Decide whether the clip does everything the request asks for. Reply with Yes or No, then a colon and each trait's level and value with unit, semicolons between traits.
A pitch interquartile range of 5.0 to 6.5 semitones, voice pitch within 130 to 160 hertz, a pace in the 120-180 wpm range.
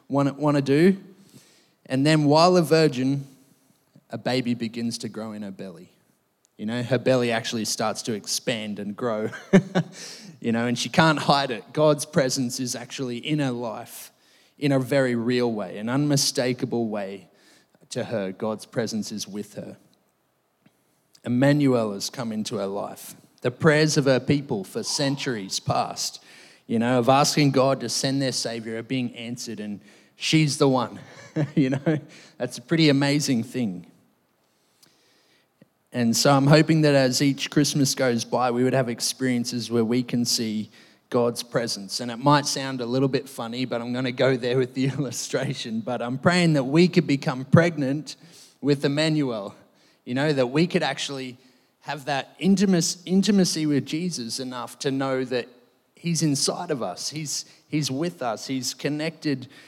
No: average, 3.8 semitones; low, 135 Hz; average, 165 wpm